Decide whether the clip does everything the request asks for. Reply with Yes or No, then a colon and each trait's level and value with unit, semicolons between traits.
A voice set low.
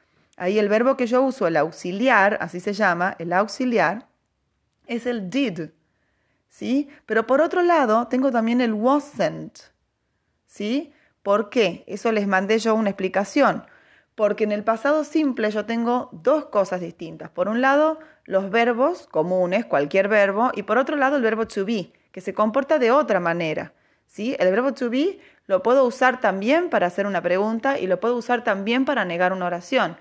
No: high, 225 Hz